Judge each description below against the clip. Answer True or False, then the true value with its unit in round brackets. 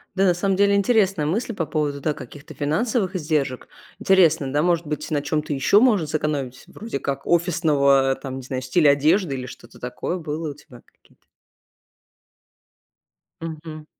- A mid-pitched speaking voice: True (155 Hz)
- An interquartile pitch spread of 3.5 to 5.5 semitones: True (4.2 semitones)